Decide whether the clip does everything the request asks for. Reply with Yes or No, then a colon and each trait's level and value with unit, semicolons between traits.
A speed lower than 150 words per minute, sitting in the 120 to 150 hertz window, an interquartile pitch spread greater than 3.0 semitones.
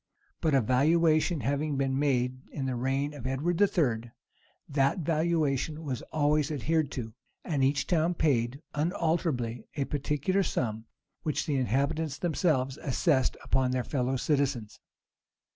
Yes: average, 140 wpm; medium, 140 Hz; average, 3.4 semitones